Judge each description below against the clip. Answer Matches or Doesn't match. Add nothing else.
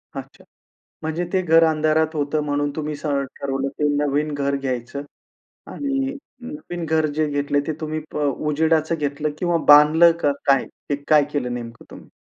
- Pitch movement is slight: Matches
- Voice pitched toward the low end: Doesn't match